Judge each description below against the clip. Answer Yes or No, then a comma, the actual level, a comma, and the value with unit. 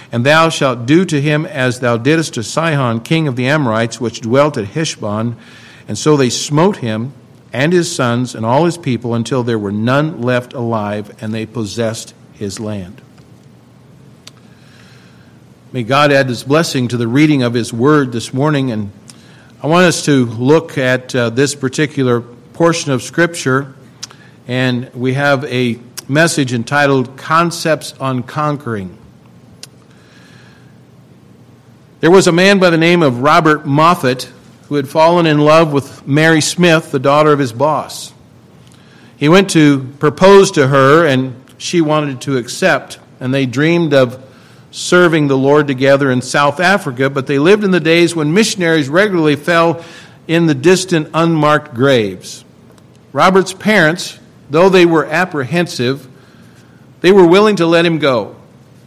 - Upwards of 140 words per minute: Yes, average, 150 wpm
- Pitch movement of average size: Yes, average, 4.5 semitones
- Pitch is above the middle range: No, medium, 140 Hz